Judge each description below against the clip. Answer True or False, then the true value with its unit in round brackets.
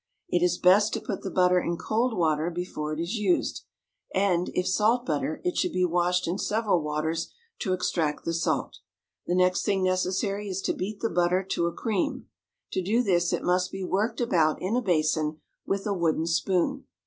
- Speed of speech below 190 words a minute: False (195 wpm)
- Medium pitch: True (180 Hz)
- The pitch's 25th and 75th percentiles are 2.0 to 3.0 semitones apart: True (2.7 semitones)